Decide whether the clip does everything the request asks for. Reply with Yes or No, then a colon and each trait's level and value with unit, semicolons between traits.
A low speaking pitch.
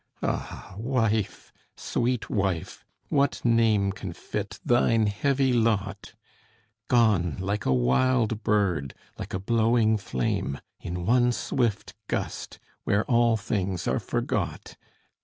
Yes: low, 110 Hz